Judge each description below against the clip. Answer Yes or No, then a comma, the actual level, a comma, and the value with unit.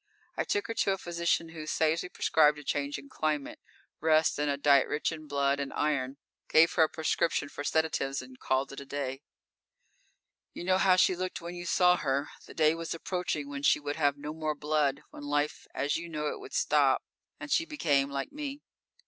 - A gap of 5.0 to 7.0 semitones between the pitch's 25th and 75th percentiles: No, average, 3.1 semitones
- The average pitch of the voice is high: No, medium, 150 Hz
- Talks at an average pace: No, fast, 210 wpm